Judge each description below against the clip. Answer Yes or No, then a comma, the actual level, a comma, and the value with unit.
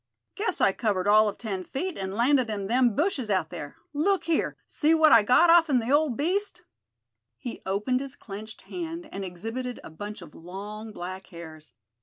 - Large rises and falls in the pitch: Yes, wide, 7.1 semitones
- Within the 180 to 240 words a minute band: Yes, average, 185 wpm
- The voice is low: No, high, 225 Hz